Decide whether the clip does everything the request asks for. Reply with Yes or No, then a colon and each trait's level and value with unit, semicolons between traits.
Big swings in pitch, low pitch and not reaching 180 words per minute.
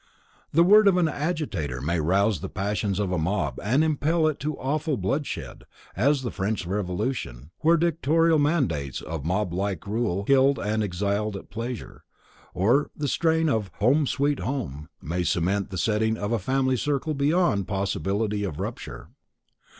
Yes: wide, 7.2 semitones; low, 110 Hz; average, 160 wpm